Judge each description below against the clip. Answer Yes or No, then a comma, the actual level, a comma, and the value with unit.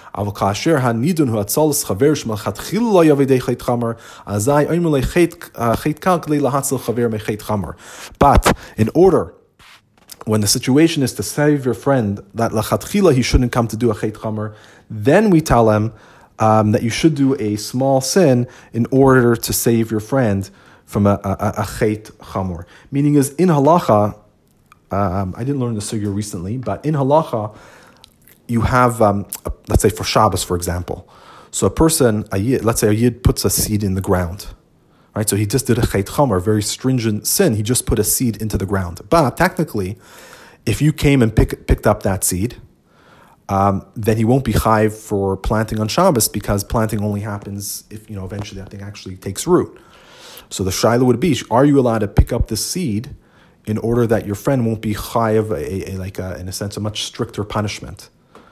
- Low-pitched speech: Yes, low, 110 Hz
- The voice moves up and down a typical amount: Yes, average, 4.0 semitones